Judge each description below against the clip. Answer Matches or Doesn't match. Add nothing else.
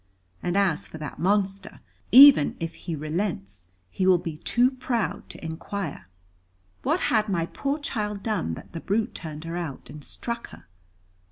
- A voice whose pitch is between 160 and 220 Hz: Matches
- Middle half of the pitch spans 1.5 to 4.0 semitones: Doesn't match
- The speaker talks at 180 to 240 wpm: Doesn't match